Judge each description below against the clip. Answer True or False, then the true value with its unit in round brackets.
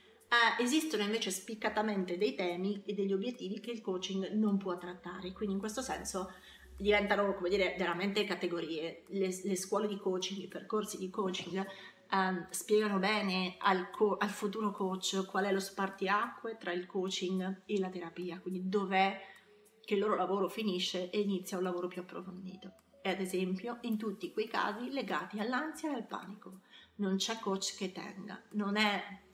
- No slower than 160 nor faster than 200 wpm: True (170 wpm)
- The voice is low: False (195 Hz)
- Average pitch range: False (2.0 semitones)